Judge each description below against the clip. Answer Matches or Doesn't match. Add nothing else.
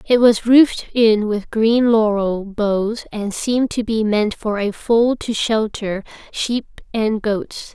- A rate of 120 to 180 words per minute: Matches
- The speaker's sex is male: Doesn't match